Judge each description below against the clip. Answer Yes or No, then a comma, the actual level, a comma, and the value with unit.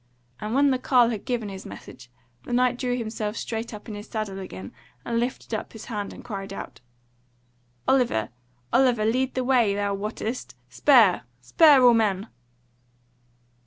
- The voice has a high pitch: Yes, high, 225 Hz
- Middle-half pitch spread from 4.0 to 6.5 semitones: No, average, 3.5 semitones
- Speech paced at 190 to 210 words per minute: No, average, 165 wpm